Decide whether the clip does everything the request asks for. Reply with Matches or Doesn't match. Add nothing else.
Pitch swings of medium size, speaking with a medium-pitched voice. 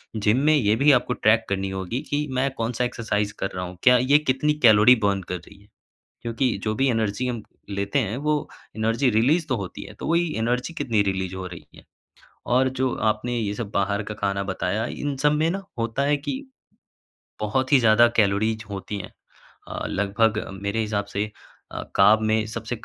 Doesn't match